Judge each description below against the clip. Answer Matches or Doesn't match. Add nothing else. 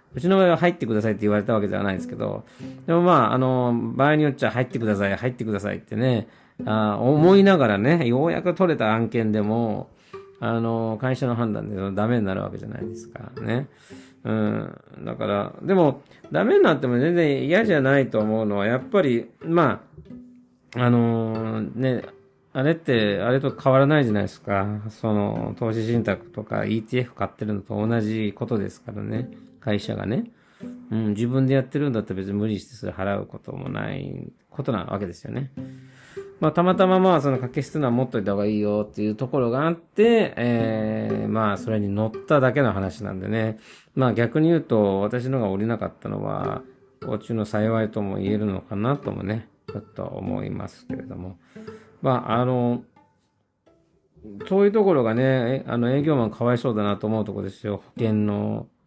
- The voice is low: Matches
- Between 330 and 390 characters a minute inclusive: Matches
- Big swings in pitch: Doesn't match